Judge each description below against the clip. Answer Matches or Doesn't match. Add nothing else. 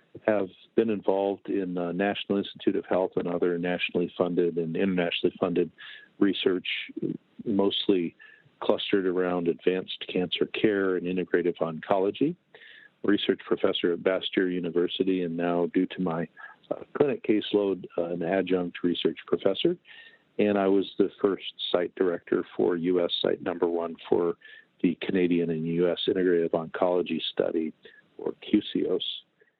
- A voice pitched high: Doesn't match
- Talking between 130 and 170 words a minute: Matches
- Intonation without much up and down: Matches